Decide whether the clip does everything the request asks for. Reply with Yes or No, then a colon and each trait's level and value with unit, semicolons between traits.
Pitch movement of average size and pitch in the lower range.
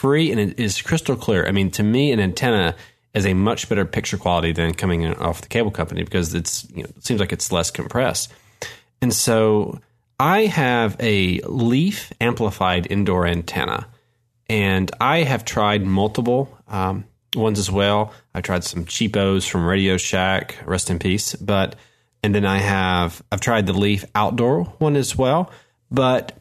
Yes: average, 4.1 semitones; low, 105 Hz